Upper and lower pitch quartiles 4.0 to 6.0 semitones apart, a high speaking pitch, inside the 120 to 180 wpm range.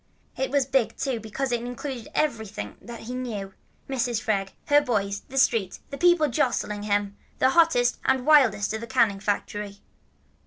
Yes: average, 4.3 semitones; high, 240 Hz; average, 170 wpm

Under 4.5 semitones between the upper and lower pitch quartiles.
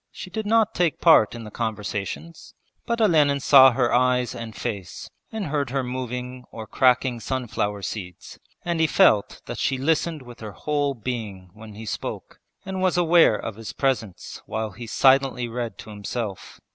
No: average, 5.2 semitones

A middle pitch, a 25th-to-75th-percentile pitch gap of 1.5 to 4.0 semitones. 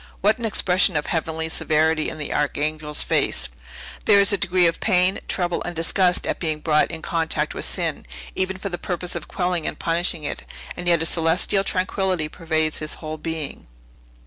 Yes: medium, 165 Hz; narrow, 2.6 semitones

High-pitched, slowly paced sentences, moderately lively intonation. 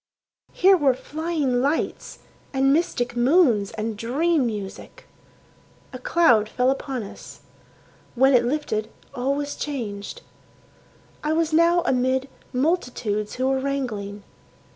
Yes: very high, 265 Hz; slow, 120 wpm; average, 4.3 semitones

